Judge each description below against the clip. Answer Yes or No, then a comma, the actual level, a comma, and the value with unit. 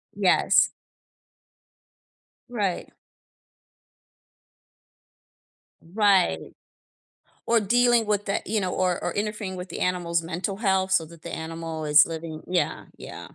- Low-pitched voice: No, medium, 185 Hz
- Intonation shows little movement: No, average, 3.8 semitones